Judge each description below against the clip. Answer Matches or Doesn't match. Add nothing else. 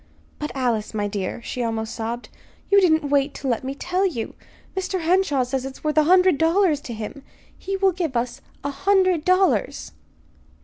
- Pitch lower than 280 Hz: Doesn't match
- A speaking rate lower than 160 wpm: Doesn't match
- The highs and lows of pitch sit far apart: Matches